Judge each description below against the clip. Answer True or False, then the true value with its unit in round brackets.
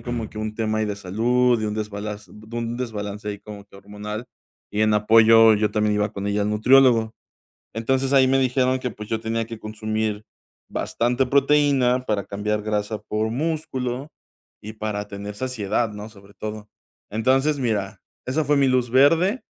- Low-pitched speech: True (110 Hz)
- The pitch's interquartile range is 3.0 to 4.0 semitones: True (3.3 semitones)